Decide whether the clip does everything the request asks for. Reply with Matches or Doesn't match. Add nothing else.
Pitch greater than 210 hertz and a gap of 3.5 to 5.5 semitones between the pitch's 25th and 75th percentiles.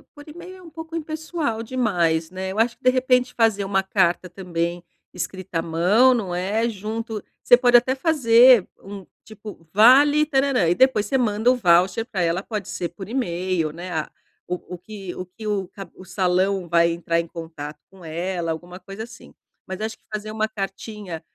Doesn't match